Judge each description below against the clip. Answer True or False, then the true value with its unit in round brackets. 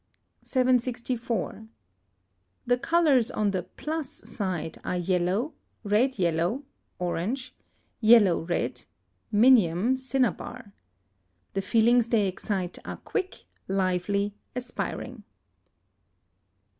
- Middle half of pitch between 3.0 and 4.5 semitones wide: False (5.3 semitones)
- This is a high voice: True (220 Hz)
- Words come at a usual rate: False (85 wpm)